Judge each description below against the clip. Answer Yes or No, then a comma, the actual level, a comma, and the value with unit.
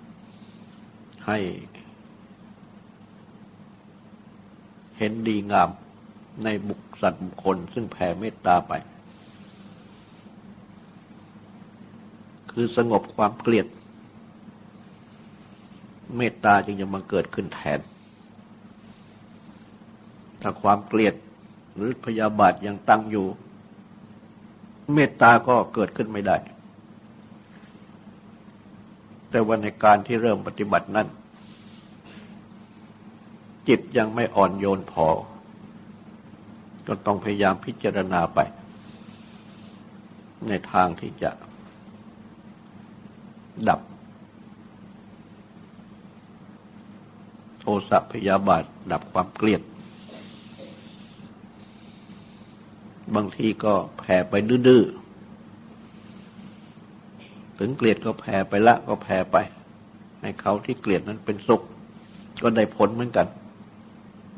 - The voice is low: Yes, low, 110 Hz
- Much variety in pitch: No, average, 3.2 semitones